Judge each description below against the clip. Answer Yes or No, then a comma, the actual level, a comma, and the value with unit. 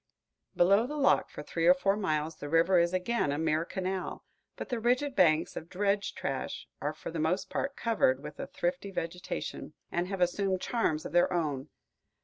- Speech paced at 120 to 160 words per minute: No, average, 190 wpm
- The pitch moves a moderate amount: Yes, average, 4.0 semitones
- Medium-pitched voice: Yes, medium, 180 Hz